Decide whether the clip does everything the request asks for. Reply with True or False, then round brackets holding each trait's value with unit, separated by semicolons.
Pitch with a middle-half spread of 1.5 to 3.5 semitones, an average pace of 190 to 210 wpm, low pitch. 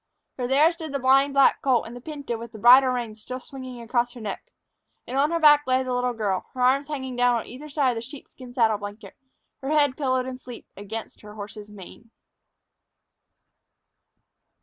False (3.0 semitones; 195 wpm; 250 Hz)